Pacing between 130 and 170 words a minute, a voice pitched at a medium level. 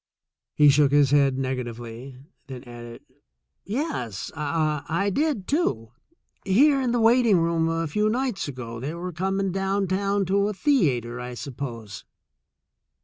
Yes: average, 145 wpm; medium, 165 Hz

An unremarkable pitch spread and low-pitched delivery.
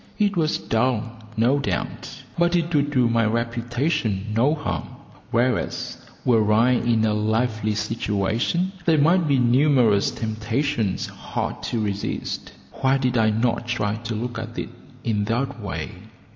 Yes: average, 3.7 semitones; low, 115 Hz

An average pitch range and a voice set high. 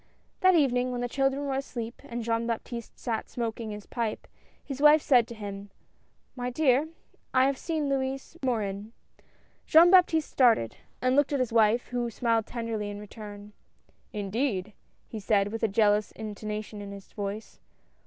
Yes: average, 3.9 semitones; high, 235 Hz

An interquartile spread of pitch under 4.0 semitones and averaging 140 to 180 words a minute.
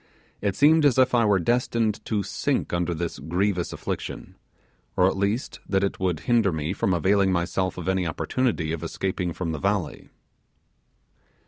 Yes: average, 3.5 semitones; average, 165 wpm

